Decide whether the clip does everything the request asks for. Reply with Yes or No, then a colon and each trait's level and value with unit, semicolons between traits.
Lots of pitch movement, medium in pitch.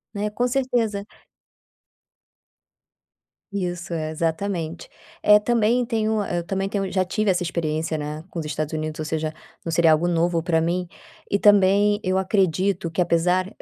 No: average, 3.7 semitones; medium, 180 Hz